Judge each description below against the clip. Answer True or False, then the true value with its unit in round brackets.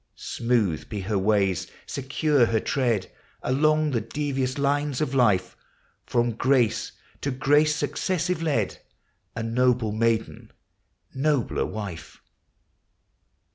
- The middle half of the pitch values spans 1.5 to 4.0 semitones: False (4.6 semitones)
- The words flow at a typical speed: False (110 wpm)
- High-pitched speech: False (125 Hz)